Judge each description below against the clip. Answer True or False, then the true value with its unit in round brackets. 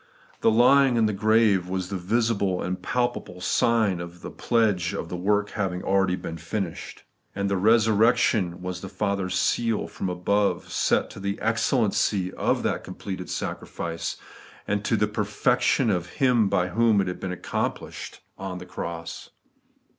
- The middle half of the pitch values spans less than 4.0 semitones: True (3.5 semitones)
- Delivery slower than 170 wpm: True (155 wpm)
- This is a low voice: True (100 Hz)